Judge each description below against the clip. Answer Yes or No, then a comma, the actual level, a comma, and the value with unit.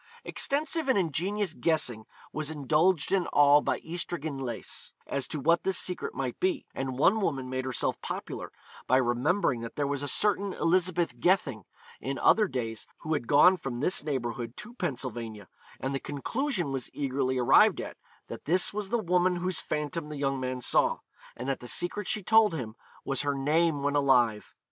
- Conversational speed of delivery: Yes, average, 175 wpm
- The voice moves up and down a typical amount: No, wide, 5.8 semitones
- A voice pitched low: No, medium, 145 Hz